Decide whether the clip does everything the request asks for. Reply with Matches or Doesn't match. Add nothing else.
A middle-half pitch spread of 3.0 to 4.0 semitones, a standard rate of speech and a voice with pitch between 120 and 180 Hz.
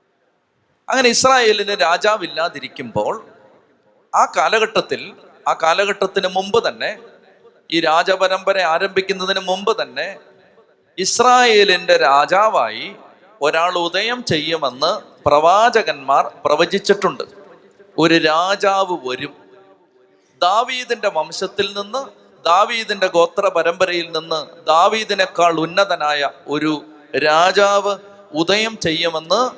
Doesn't match